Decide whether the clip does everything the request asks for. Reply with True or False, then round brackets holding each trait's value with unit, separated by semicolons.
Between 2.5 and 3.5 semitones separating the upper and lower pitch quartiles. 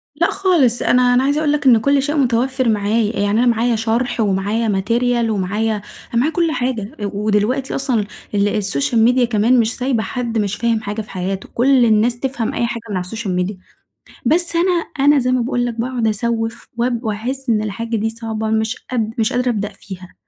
True (2.9 semitones)